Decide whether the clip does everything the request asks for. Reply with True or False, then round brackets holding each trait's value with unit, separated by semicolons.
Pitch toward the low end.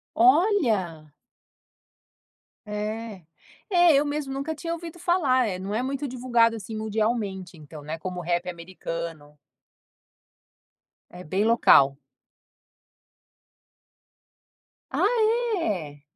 False (215 Hz)